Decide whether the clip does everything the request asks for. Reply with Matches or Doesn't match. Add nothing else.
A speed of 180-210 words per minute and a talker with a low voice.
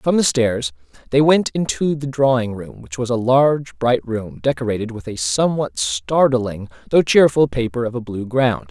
Matches